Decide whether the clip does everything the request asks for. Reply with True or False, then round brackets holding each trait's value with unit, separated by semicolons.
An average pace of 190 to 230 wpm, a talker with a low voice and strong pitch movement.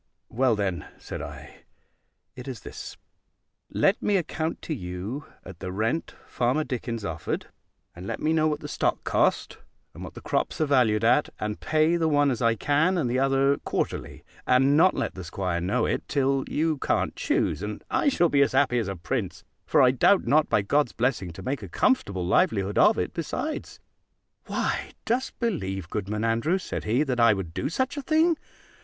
True (195 wpm; 130 Hz; 6.9 semitones)